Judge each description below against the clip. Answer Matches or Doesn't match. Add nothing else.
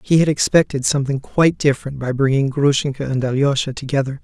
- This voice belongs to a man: Matches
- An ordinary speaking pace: Matches